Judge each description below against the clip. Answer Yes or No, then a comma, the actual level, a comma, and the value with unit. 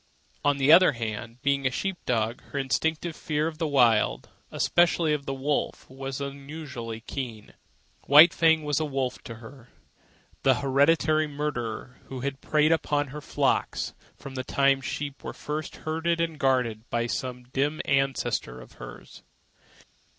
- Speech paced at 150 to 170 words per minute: Yes, average, 160 wpm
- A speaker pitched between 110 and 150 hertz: Yes, medium, 140 Hz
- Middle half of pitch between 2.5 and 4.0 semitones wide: Yes, average, 3.2 semitones